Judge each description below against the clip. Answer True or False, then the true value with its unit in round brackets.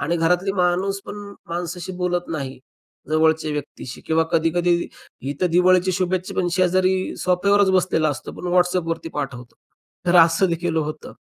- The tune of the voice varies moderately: False (2.3 semitones)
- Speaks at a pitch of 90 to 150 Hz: False (175 Hz)